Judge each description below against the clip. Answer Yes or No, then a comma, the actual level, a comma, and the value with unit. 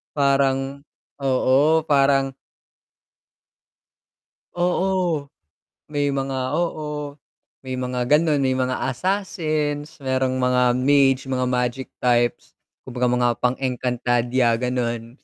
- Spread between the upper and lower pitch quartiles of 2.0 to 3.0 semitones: Yes, narrow, 2.6 semitones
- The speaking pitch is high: No, low, 135 Hz